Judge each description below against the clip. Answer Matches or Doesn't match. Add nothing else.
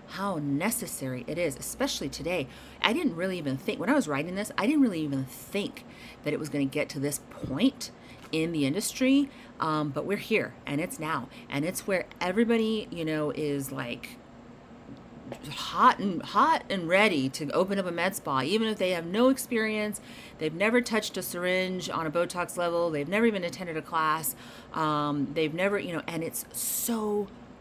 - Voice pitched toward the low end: Doesn't match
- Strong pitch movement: Matches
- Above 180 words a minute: Matches